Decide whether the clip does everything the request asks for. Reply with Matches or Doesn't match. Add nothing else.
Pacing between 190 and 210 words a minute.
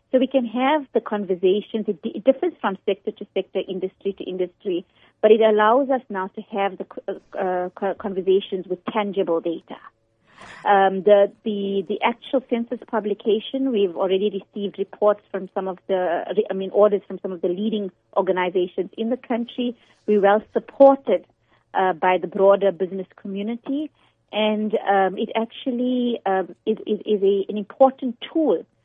Doesn't match